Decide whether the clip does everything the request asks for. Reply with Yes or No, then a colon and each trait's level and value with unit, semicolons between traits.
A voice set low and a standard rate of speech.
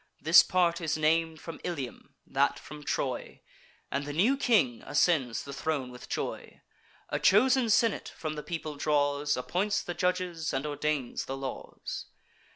No: medium, 155 Hz; average, 155 wpm